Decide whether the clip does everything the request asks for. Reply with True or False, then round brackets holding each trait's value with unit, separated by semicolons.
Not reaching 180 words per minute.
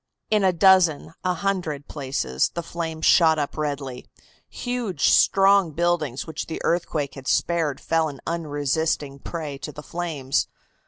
True (145 wpm)